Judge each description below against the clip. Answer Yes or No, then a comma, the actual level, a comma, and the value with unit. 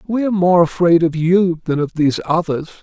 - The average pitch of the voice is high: No, medium, 170 Hz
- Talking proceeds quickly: Yes, fast, 210 wpm